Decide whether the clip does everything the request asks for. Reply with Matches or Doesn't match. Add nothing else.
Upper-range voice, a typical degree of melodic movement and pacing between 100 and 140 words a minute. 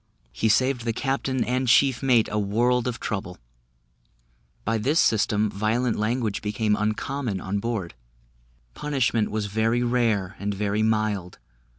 Doesn't match